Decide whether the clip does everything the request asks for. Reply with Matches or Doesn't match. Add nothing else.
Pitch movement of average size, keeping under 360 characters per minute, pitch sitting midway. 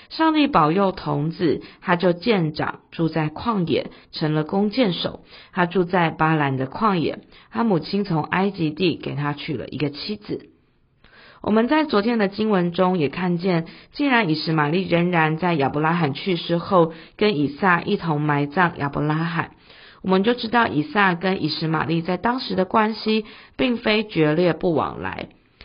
Matches